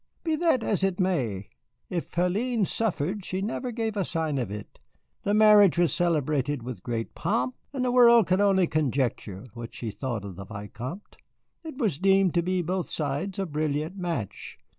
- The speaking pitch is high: No, medium, 175 Hz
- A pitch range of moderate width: No, wide, 7.5 semitones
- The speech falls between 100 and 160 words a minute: No, average, 175 wpm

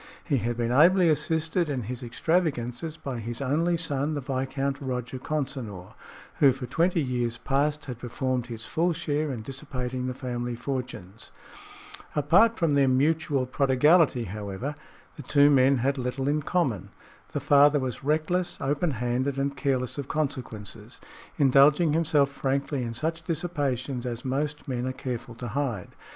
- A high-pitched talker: No, low, 135 Hz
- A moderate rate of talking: Yes, average, 155 wpm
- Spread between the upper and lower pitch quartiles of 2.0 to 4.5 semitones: Yes, average, 3.2 semitones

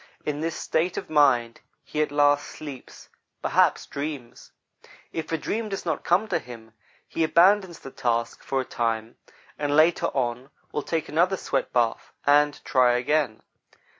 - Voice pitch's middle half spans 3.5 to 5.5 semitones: Yes, average, 4.9 semitones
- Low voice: No, medium, 145 Hz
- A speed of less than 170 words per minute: Yes, average, 155 wpm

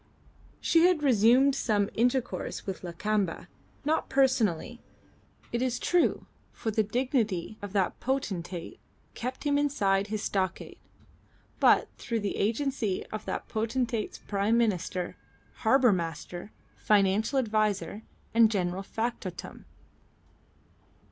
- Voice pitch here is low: No, high, 220 Hz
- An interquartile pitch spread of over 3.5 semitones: Yes, average, 4.4 semitones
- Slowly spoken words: Yes, slow, 110 wpm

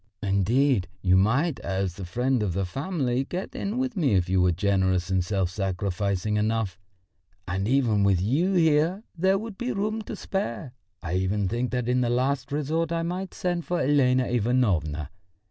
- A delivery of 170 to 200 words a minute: Yes, average, 180 wpm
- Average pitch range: No, wide, 8.4 semitones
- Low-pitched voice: Yes, low, 120 Hz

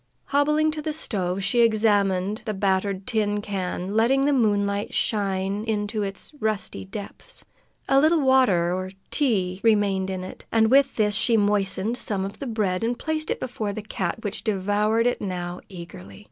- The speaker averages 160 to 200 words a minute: Yes, average, 170 wpm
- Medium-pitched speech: No, high, 205 Hz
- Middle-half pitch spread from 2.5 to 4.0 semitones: Yes, average, 3.4 semitones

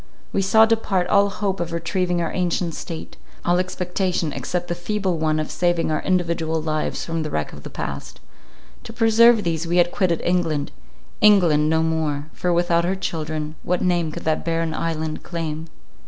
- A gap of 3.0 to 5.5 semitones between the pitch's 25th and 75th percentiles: No, narrow, 2.4 semitones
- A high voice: No, medium, 170 Hz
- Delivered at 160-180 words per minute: Yes, average, 170 wpm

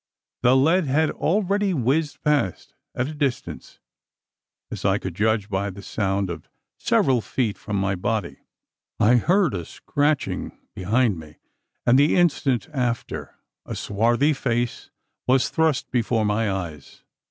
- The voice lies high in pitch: No, low, 120 Hz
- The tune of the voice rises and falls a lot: Yes, wide, 6.4 semitones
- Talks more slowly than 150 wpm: Yes, average, 140 wpm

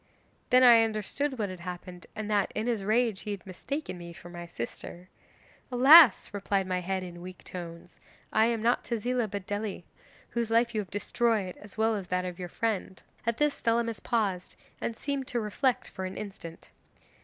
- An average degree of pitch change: Yes, average, 4.2 semitones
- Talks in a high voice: Yes, high, 210 Hz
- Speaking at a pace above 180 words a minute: Yes, average, 190 wpm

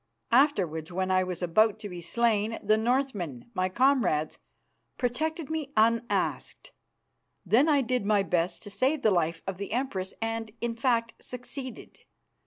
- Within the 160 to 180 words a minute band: No, average, 150 wpm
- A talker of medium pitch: No, high, 225 Hz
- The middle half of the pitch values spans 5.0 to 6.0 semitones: Yes, average, 5.3 semitones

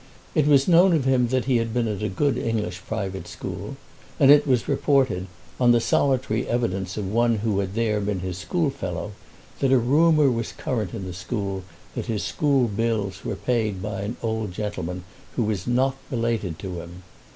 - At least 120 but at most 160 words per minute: No, average, 190 wpm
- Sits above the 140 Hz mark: No, low, 115 Hz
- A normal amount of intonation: Yes, average, 4.8 semitones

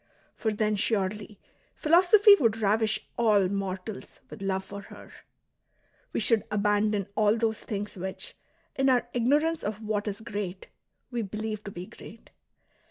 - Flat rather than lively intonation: Yes, narrow, 2.2 semitones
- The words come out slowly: No, average, 145 wpm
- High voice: Yes, high, 210 Hz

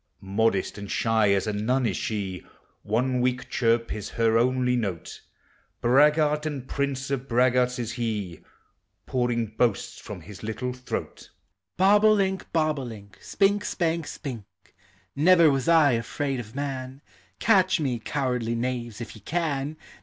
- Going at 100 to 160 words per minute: Yes, average, 150 wpm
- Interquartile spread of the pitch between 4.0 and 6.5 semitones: Yes, average, 4.3 semitones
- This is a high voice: No, low, 125 Hz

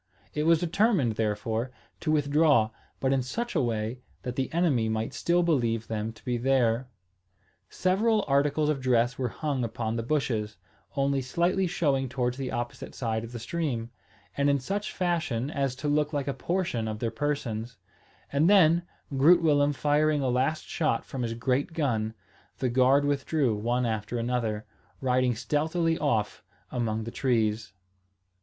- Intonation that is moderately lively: Yes, average, 4.7 semitones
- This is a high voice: No, low, 130 Hz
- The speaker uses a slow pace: No, average, 165 wpm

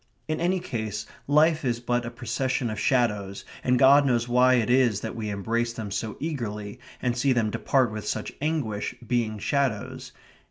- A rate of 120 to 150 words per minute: No, average, 175 wpm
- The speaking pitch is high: No, low, 120 Hz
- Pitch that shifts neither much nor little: Yes, average, 3.3 semitones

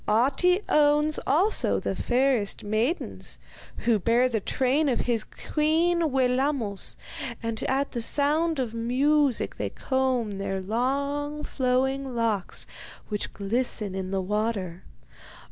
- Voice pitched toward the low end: No, very high, 255 Hz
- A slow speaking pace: Yes, slow, 120 wpm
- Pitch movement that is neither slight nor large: Yes, average, 4.8 semitones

